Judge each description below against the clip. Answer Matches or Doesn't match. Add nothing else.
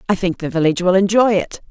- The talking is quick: Matches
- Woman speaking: Matches